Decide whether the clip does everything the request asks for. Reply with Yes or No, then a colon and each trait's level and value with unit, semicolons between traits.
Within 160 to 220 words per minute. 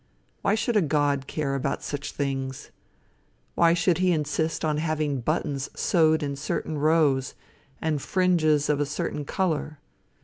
No: average, 145 wpm